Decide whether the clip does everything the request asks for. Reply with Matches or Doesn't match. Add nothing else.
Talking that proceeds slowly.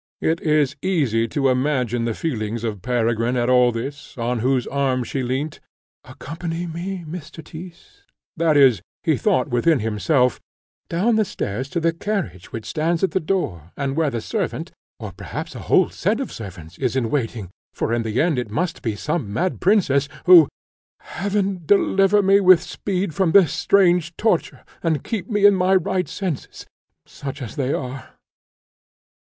Doesn't match